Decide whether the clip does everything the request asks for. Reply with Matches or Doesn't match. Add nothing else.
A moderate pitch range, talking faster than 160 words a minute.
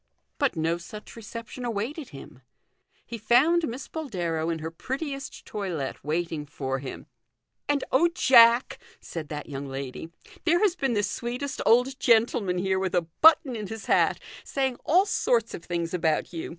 Doesn't match